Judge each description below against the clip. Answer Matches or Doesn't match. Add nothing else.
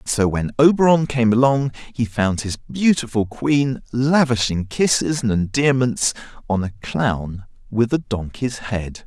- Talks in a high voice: Doesn't match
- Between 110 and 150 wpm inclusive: Matches